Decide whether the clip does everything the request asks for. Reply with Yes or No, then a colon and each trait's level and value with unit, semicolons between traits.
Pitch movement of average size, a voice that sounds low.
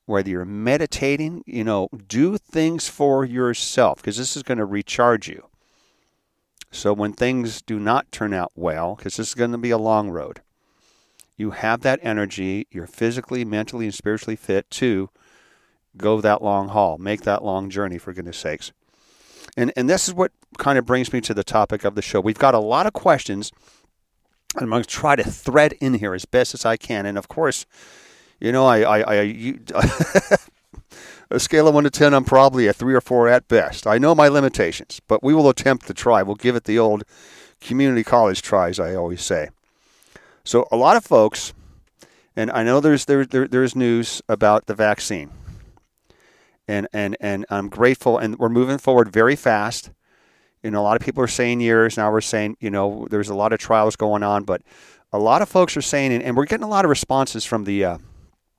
Yes: average, 4.1 semitones; low, 115 Hz